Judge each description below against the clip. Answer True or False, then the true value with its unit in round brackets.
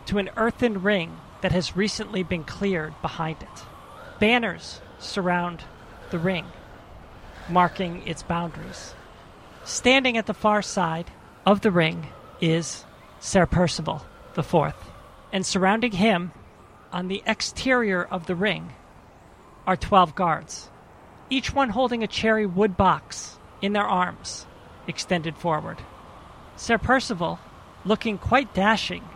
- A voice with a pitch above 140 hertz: True (185 Hz)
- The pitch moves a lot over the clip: False (4.4 semitones)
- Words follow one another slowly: True (125 wpm)